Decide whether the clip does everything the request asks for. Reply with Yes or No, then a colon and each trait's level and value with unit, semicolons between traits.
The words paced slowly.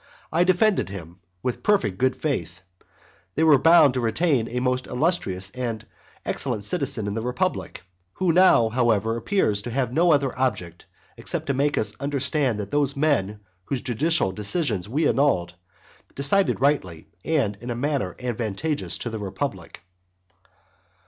No: average, 150 wpm